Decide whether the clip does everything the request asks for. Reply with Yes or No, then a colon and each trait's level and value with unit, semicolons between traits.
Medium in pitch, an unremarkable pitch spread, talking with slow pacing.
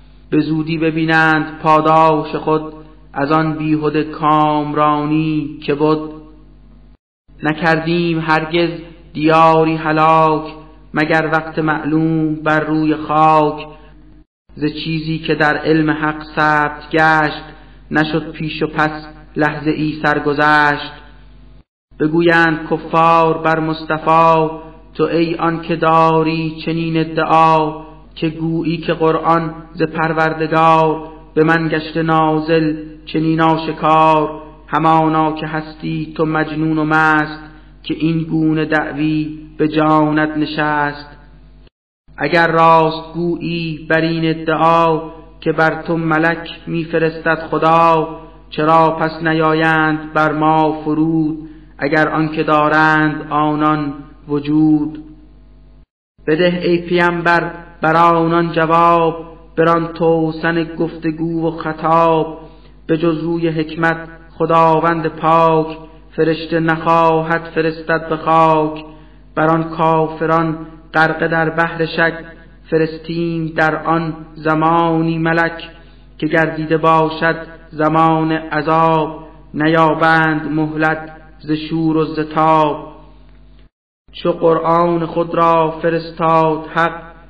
No: medium, 160 Hz; narrow, 0.9 semitones; slow, 100 wpm